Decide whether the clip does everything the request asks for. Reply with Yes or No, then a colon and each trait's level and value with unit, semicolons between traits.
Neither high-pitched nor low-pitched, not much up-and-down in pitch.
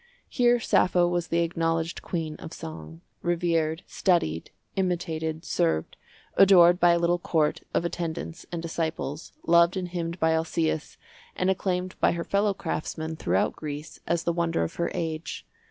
Yes: medium, 170 Hz; narrow, 1.7 semitones